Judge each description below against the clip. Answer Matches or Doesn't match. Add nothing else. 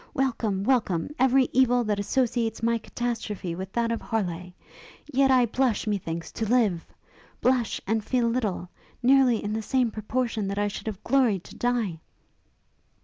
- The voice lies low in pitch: Doesn't match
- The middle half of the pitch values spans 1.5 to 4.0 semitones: Matches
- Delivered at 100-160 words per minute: Matches